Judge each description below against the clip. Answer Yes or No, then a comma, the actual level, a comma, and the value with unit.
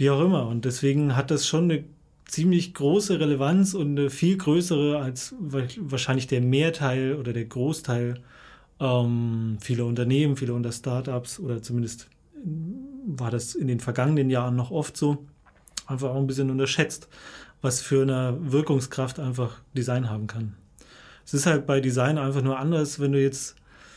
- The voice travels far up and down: No, average, 3.3 semitones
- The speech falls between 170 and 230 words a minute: No, average, 160 wpm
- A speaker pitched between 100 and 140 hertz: Yes, low, 135 Hz